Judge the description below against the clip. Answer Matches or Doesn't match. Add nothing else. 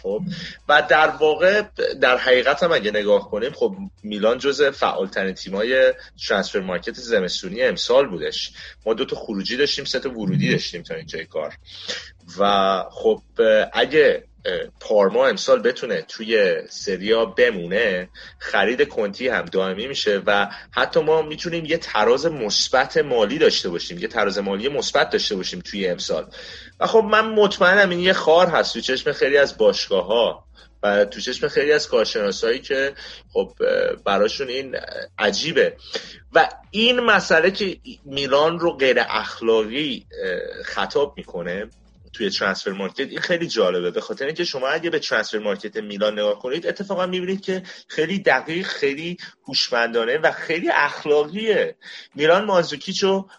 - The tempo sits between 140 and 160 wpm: Matches